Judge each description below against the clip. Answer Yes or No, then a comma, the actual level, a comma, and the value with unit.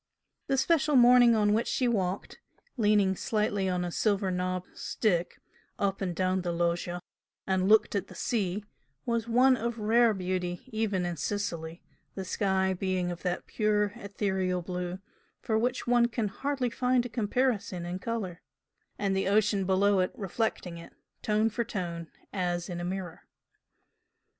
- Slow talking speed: No, average, 155 wpm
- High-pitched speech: Yes, high, 195 Hz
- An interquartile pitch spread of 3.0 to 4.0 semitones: Yes, average, 3.7 semitones